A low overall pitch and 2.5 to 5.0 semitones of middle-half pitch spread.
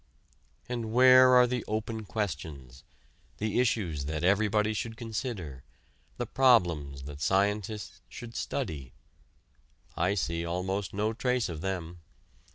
No: low, 100 Hz; wide, 5.5 semitones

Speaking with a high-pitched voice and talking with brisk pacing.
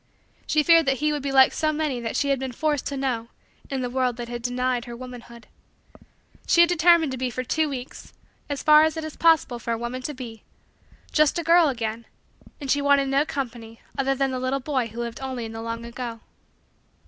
Yes: very high, 260 Hz; fast, 220 wpm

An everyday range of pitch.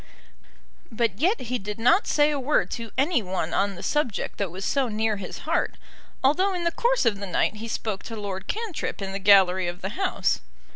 No: wide, 7.2 semitones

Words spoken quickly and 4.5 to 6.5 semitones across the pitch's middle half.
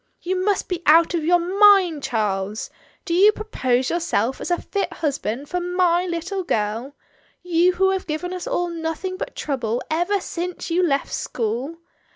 No: average, 175 wpm; average, 4.8 semitones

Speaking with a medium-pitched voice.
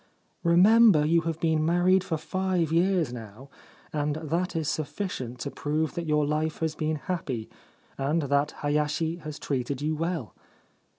Yes: medium, 155 Hz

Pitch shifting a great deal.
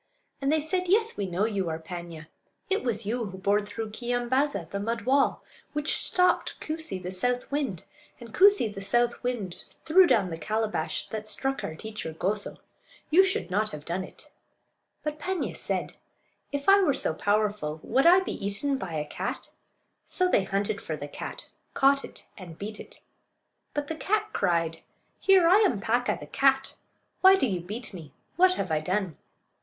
Yes: wide, 7.6 semitones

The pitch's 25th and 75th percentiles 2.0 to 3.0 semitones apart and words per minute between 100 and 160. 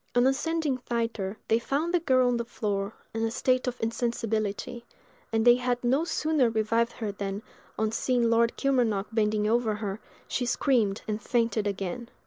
No: narrow, 2.6 semitones; average, 170 wpm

